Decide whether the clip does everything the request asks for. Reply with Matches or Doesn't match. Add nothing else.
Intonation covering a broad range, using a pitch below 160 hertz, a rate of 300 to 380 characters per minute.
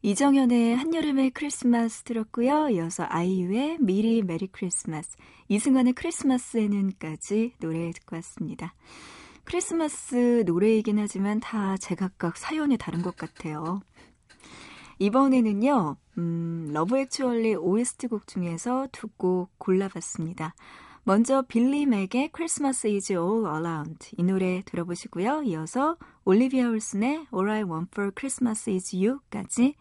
Doesn't match